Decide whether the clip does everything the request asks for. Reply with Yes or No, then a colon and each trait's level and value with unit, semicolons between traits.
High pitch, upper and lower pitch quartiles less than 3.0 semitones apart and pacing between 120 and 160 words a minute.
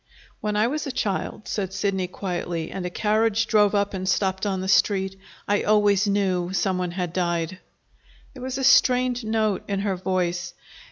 No: high, 195 Hz; narrow, 2.5 semitones; average, 180 wpm